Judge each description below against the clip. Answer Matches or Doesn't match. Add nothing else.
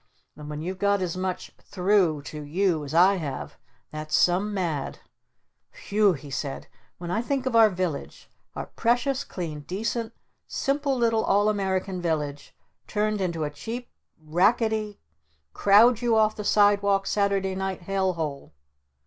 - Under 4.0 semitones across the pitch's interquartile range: Doesn't match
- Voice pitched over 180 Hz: Matches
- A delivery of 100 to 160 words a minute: Matches